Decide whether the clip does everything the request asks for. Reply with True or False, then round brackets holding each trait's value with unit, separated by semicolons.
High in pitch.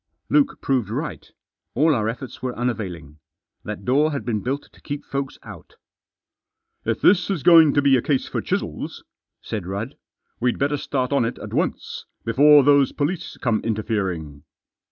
False (130 Hz)